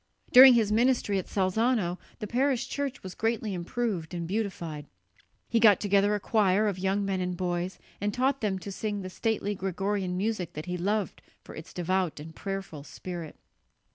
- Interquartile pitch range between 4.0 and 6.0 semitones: No, average, 3.4 semitones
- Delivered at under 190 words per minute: Yes, average, 175 wpm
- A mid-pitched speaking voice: No, high, 195 Hz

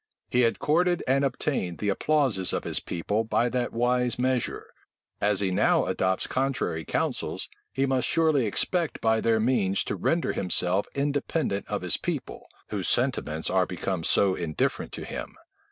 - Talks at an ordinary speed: Yes, average, 160 wpm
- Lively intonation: Yes, wide, 6.1 semitones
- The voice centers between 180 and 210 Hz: No, low, 115 Hz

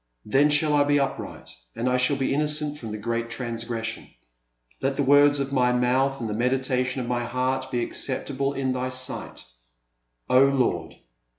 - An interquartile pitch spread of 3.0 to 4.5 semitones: No, narrow, 2.4 semitones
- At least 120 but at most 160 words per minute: No, average, 180 wpm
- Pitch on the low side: Yes, low, 130 Hz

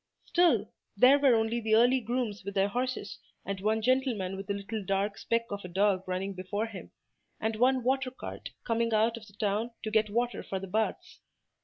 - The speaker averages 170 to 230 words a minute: Yes, average, 200 wpm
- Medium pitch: No, high, 220 Hz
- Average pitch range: Yes, average, 3.3 semitones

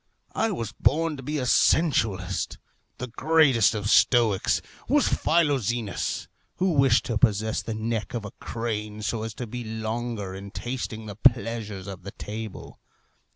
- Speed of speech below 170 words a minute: Yes, average, 155 wpm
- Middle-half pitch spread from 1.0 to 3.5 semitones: Yes, average, 3.1 semitones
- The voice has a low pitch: Yes, low, 115 Hz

